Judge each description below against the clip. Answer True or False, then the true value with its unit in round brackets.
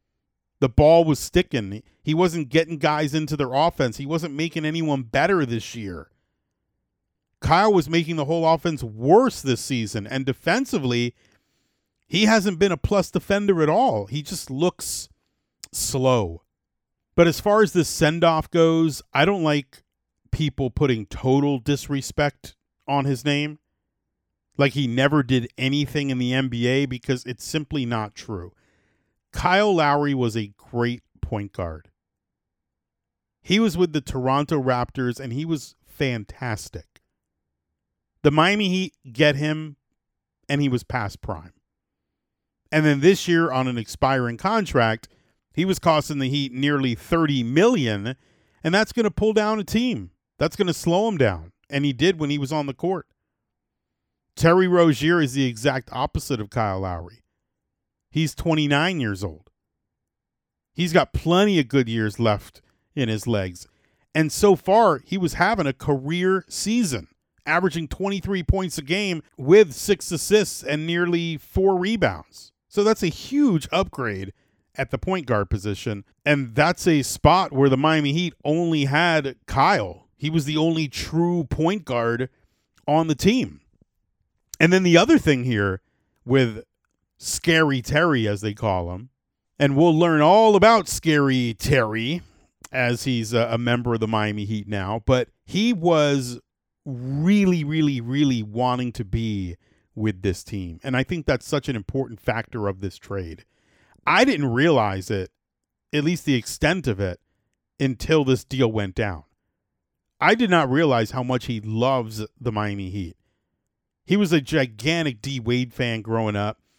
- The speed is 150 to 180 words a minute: True (155 wpm)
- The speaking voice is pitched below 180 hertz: True (140 Hz)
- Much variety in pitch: True (6.3 semitones)